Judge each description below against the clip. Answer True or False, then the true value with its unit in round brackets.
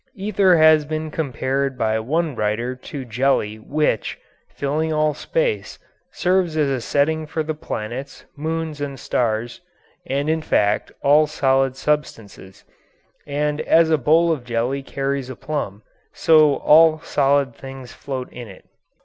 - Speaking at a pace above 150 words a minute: False (140 wpm)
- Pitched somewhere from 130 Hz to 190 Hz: True (140 Hz)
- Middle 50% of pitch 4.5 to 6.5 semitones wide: False (3.6 semitones)